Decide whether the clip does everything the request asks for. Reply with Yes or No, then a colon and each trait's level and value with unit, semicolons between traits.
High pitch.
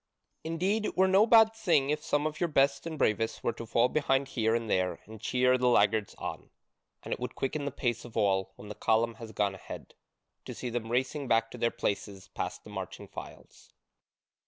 No: low, 125 Hz